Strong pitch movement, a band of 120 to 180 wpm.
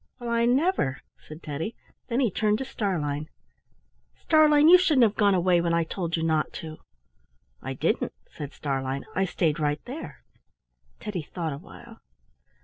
Yes: wide, 7.4 semitones; average, 155 wpm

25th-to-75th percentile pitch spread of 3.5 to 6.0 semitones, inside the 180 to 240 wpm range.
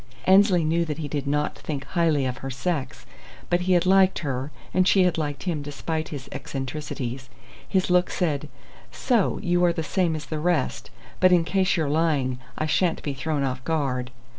Yes: average, 4.1 semitones; average, 190 wpm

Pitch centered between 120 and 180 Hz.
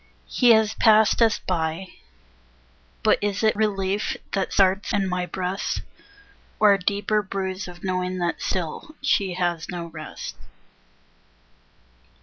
No: high, 190 Hz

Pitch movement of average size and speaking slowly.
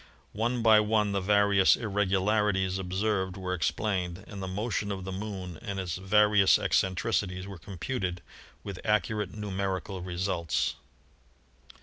No: narrow, 2.1 semitones; slow, 125 wpm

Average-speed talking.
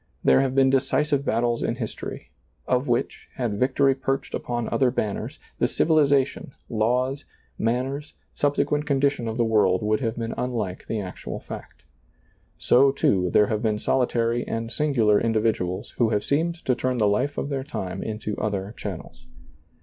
Yes: average, 165 wpm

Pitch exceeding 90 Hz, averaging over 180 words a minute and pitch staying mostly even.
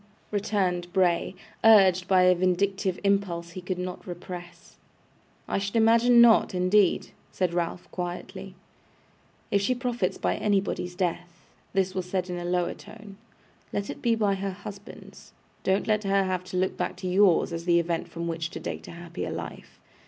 No: medium, 185 Hz; average, 170 wpm; narrow, 2.2 semitones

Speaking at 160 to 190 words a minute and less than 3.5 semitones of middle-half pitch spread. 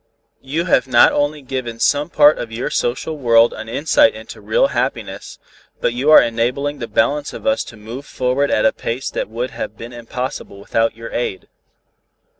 No: average, 185 wpm; average, 3.8 semitones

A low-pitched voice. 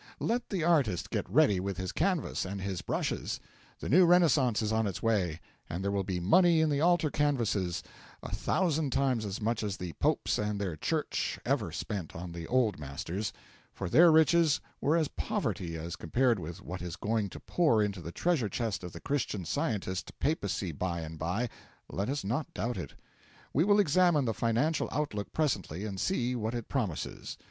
Yes: low, 110 Hz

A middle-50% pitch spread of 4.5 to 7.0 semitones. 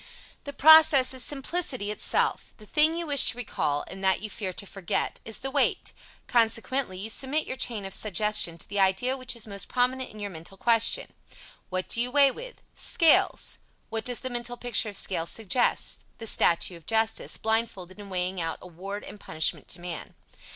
Yes: average, 5.1 semitones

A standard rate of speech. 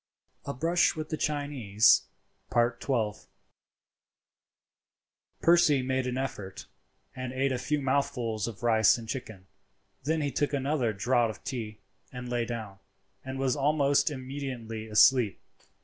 No: slow, 125 wpm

